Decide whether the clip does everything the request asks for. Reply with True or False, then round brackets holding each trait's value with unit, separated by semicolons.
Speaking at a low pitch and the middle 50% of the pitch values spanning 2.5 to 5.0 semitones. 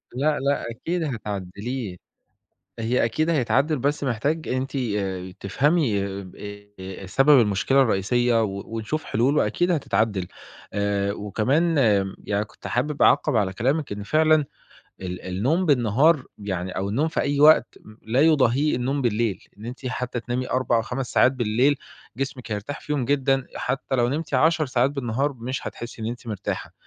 False (125 Hz; 5.4 semitones)